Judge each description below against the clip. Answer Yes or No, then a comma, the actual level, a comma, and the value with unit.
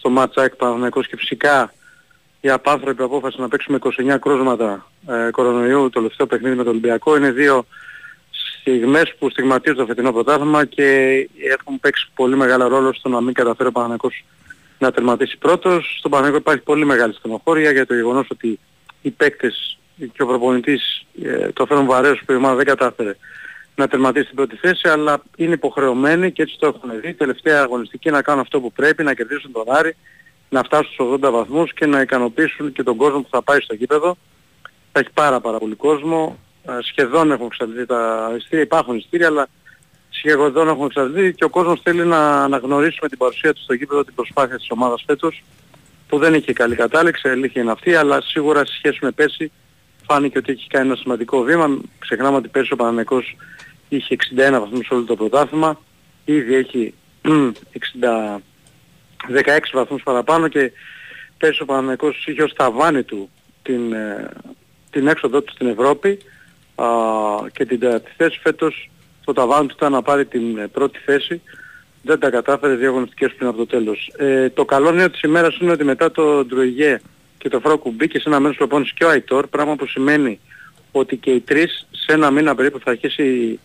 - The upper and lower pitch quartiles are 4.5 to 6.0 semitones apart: No, average, 3.3 semitones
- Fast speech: Yes, fast, 180 wpm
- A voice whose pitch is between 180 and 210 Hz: No, low, 135 Hz